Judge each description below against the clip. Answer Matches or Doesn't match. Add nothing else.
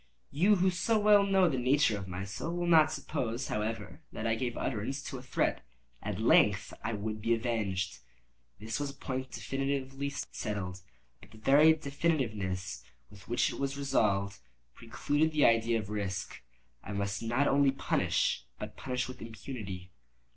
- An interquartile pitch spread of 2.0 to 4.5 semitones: Doesn't match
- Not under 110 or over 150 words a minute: Doesn't match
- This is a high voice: Doesn't match